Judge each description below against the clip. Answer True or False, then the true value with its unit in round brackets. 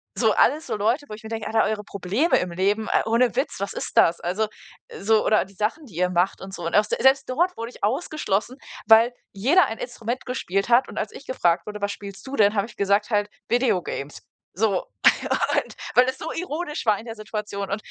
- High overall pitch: True (215 Hz)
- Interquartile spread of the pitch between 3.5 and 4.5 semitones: True (3.9 semitones)